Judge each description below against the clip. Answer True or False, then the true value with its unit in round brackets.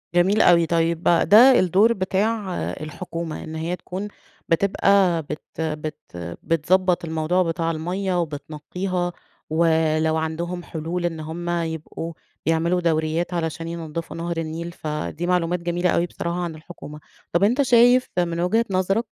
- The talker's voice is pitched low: False (170 Hz)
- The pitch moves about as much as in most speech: False (2.1 semitones)